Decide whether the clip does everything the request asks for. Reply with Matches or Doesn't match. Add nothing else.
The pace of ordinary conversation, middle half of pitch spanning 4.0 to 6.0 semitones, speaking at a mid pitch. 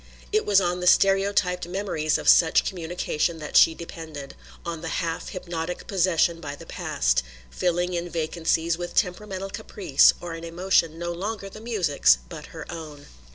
Doesn't match